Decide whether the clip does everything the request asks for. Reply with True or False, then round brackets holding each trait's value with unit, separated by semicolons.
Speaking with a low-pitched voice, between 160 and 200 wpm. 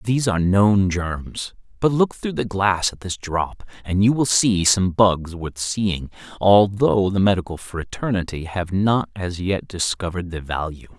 True (95 Hz; 170 wpm)